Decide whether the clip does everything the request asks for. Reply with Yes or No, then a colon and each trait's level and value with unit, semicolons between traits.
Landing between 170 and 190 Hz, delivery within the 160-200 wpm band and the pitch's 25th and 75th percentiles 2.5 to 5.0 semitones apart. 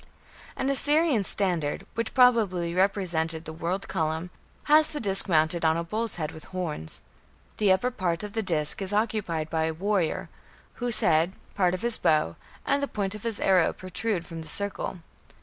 Yes: medium, 185 Hz; average, 180 wpm; average, 4.7 semitones